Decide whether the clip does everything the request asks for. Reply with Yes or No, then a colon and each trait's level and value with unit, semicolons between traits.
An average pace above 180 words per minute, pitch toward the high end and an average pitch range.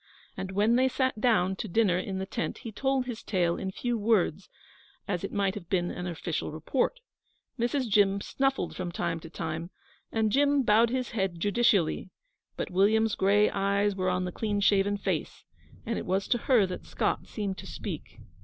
Yes: average, 190 wpm; high, 200 Hz; average, 3.8 semitones